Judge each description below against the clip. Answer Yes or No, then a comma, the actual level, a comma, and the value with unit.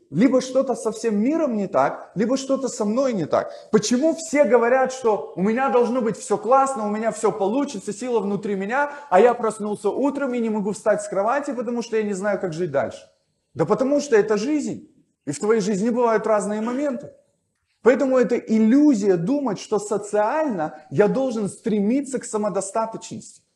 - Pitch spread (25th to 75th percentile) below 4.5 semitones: Yes, average, 3.9 semitones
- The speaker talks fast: Yes, fast, 180 wpm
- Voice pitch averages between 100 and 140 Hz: No, high, 220 Hz